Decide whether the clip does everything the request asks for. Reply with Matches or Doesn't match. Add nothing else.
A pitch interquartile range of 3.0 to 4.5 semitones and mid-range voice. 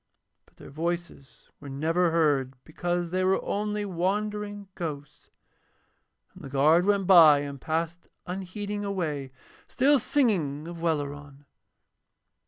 Doesn't match